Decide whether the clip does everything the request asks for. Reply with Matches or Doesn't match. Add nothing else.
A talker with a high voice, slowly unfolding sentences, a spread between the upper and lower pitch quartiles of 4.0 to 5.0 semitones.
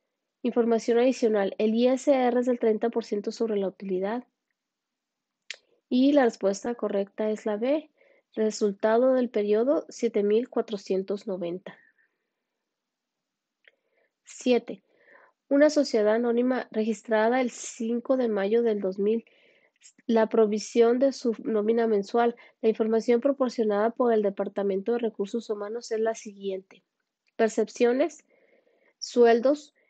Doesn't match